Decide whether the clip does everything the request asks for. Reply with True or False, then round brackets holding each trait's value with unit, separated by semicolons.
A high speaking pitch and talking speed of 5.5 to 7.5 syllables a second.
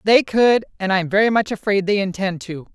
False (200 Hz; 5.3 syllables/s)